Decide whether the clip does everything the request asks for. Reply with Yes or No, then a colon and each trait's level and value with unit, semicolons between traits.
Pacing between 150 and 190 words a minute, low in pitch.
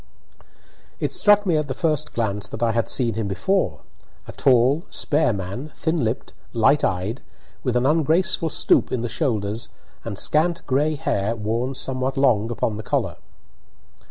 Yes: average, 155 wpm; low, 125 Hz